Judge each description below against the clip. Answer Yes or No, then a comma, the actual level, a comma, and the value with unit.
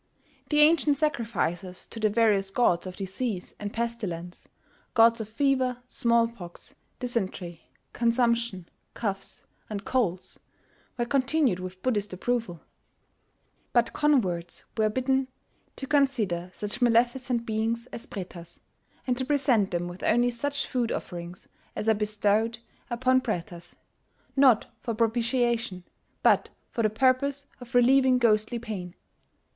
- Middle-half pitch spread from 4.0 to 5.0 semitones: Yes, average, 4.4 semitones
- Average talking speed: No, slow, 125 wpm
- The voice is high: Yes, high, 230 Hz